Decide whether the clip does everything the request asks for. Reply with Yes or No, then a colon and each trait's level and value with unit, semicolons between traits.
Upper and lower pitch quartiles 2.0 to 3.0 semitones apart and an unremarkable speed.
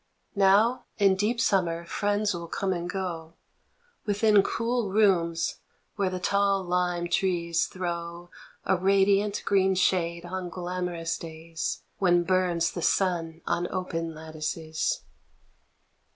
No: narrow, 2.5 semitones; slow, 130 wpm